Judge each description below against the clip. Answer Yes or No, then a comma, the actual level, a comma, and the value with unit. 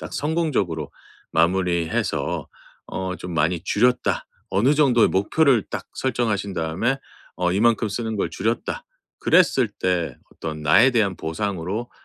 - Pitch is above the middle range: No, low, 100 Hz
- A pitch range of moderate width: No, wide, 5.8 semitones